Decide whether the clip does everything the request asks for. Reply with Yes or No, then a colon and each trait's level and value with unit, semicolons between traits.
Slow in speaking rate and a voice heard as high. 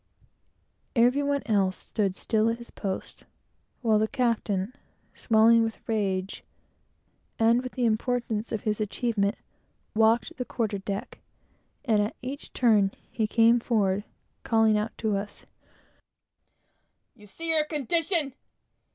Yes: slow, 130 wpm; high, 225 Hz